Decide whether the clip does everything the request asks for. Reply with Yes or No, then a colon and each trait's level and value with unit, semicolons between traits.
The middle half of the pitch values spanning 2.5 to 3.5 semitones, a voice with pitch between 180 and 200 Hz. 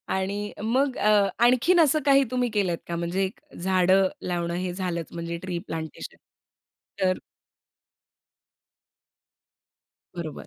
No: average, 4.0 semitones; high, 190 Hz